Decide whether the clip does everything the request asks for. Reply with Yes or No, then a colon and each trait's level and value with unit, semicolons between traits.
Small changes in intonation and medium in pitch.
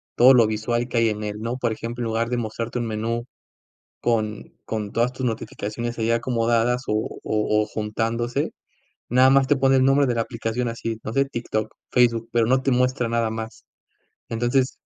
No: narrow, 1.7 semitones; low, 115 Hz